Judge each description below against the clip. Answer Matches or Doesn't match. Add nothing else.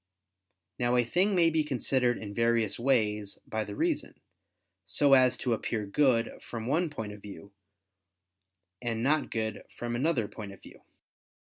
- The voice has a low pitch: Matches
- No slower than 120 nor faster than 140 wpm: Doesn't match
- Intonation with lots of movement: Doesn't match